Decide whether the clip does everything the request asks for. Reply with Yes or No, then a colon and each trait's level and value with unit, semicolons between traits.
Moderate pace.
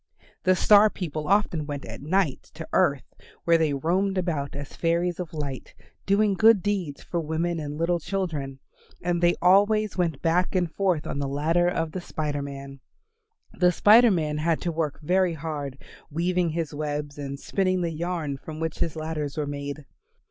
Yes: average, 175 wpm